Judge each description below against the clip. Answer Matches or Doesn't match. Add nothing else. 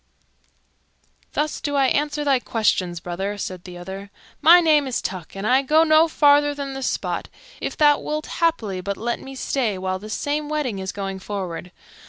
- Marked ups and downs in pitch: Matches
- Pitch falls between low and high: Doesn't match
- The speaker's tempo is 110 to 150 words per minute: Doesn't match